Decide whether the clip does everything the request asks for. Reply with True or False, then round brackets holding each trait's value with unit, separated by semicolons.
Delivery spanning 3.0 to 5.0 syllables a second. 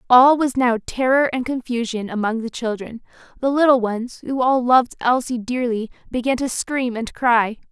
True (4.8 syllables/s)